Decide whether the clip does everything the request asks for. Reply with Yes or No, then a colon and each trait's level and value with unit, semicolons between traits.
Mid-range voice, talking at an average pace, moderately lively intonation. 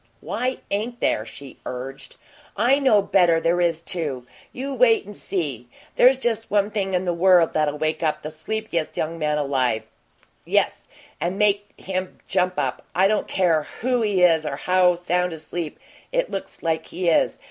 Yes: medium, 180 Hz; average, 180 wpm; average, 4.8 semitones